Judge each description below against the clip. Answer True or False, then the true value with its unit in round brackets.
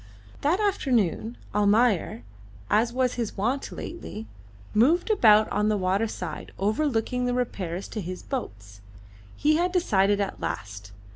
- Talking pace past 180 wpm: False (135 wpm)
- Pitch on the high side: True (220 Hz)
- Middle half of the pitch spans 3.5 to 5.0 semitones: True (4.6 semitones)